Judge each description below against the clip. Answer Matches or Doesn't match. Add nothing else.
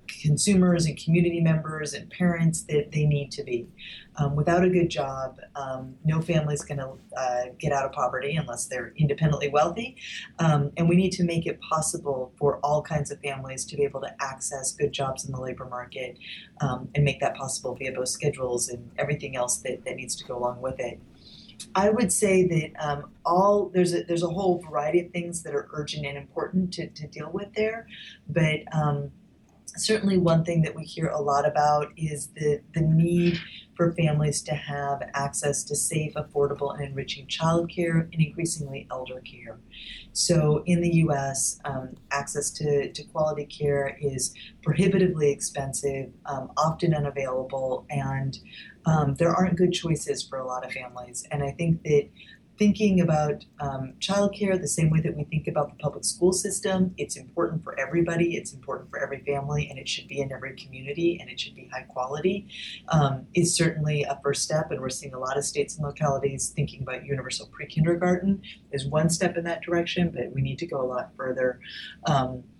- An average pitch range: Matches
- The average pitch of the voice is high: Doesn't match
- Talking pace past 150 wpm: Matches